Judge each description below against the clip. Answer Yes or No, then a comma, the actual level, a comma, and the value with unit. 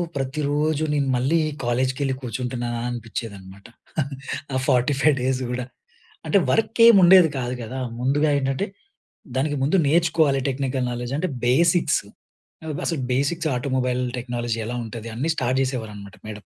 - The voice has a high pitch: No, low, 130 Hz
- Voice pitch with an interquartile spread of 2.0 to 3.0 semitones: No, average, 3.4 semitones